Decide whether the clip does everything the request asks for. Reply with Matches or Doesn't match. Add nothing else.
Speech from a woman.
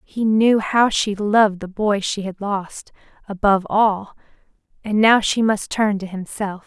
Matches